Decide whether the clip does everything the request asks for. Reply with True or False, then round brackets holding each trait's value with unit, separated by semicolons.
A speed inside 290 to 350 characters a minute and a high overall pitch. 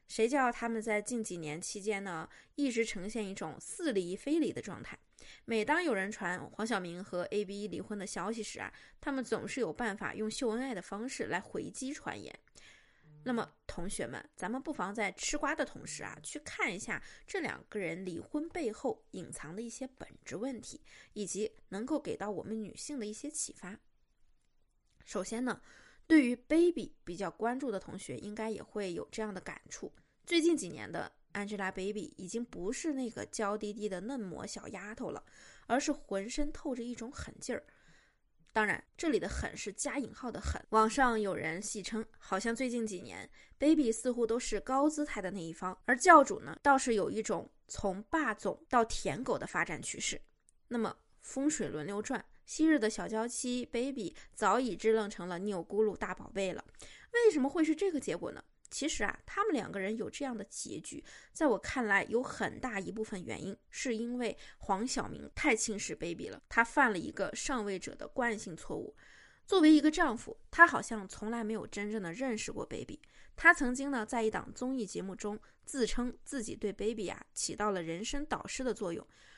True (295 characters per minute; 225 Hz)